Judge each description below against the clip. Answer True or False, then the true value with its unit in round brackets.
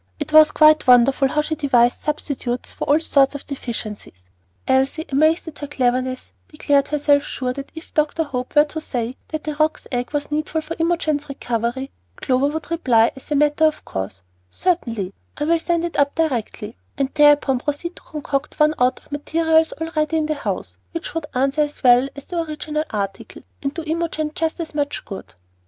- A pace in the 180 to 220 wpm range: True (190 wpm)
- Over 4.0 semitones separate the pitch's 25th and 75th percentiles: False (3.2 semitones)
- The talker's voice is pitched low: False (290 Hz)